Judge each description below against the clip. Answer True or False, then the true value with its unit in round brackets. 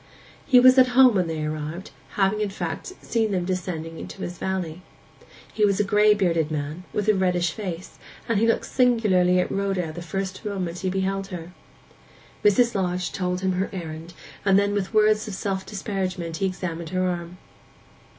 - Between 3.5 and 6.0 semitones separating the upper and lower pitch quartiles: False (2.8 semitones)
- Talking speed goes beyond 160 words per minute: True (180 wpm)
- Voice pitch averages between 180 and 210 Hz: True (190 Hz)